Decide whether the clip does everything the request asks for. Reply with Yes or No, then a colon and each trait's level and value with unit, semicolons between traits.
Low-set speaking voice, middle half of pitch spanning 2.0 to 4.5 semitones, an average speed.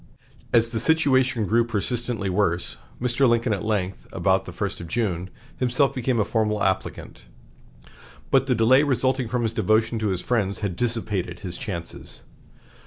Yes: low, 115 Hz; average, 3.6 semitones; average, 160 wpm